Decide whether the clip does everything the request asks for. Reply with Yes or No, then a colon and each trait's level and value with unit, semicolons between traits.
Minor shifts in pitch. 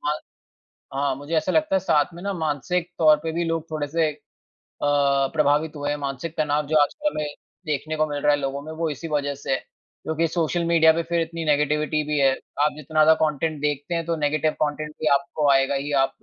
Yes: narrow, 2.1 semitones